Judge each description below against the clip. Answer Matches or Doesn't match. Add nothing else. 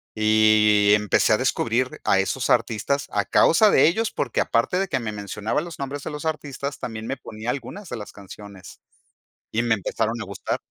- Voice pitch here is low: Matches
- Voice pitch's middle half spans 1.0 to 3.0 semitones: Doesn't match